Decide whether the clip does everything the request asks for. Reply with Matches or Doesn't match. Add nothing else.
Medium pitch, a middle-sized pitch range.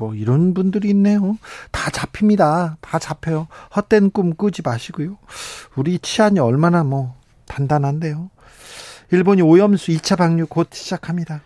Matches